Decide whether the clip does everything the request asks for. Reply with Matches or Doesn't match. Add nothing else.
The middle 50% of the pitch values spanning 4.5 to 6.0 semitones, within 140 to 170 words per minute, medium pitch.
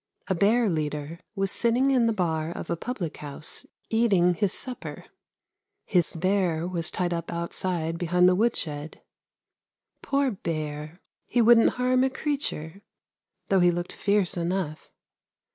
Matches